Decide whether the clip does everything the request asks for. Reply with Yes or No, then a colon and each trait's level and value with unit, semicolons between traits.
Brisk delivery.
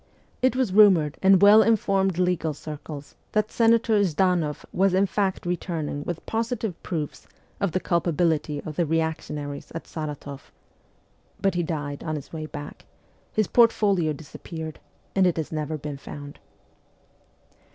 No: average, 140 wpm